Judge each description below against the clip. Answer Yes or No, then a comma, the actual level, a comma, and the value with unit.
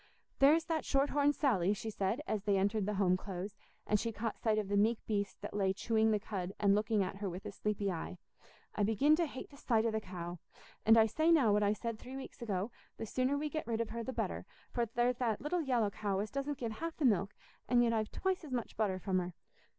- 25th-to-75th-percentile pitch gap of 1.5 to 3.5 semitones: No, average, 4.1 semitones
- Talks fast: Yes, fast, 250 wpm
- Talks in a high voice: Yes, high, 220 Hz